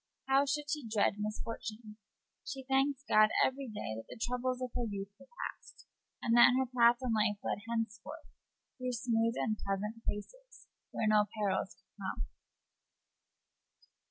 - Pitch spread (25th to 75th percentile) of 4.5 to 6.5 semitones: No, average, 3.8 semitones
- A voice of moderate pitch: No, high, 230 Hz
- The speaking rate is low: No, average, 155 wpm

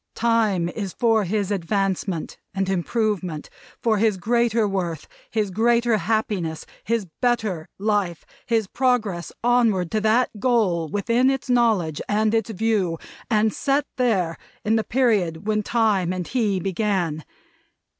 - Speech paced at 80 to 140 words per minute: Yes, slow, 135 wpm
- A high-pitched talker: Yes, high, 210 Hz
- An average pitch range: Yes, average, 3.8 semitones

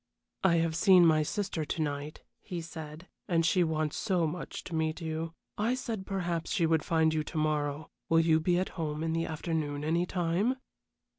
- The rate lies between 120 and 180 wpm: No, average, 195 wpm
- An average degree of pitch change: No, narrow, 2.0 semitones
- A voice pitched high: No, medium, 165 Hz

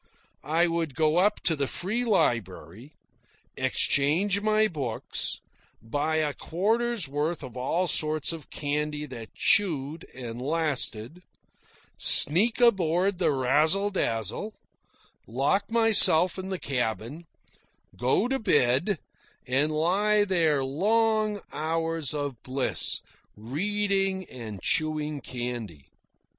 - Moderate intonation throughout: No, wide, 6.5 semitones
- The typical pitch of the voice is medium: Yes, medium, 155 Hz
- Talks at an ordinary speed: No, slow, 110 wpm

